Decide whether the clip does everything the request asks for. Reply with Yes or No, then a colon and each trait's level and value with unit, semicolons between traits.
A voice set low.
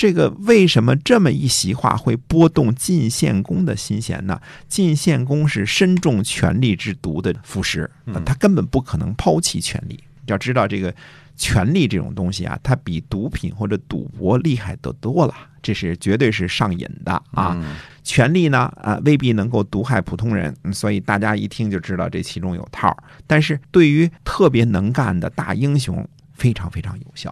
Yes: low, 120 Hz